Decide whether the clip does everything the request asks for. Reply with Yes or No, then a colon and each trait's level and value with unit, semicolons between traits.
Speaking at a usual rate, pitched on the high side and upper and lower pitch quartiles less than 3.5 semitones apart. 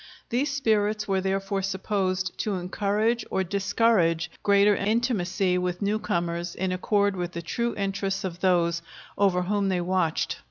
Yes: average, 145 wpm; high, 195 Hz; narrow, 2.4 semitones